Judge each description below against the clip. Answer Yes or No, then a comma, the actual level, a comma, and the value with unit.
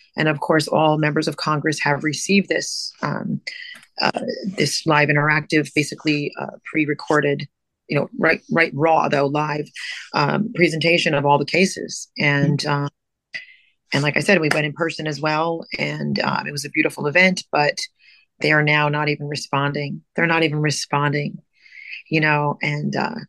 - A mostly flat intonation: Yes, narrow, 1.9 semitones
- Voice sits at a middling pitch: Yes, medium, 150 Hz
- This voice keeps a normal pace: Yes, average, 165 wpm